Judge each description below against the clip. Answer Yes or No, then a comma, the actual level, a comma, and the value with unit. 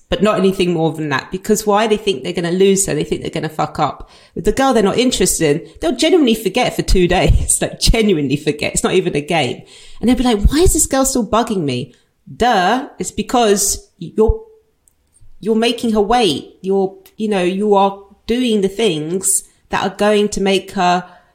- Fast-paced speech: Yes, fast, 215 wpm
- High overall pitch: Yes, high, 195 Hz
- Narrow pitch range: No, average, 3.8 semitones